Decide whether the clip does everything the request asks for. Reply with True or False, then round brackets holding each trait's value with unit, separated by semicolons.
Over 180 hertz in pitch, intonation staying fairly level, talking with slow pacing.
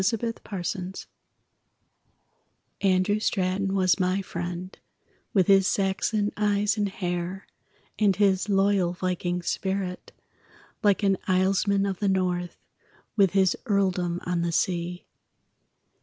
True (190 Hz; 1.8 semitones; 115 wpm)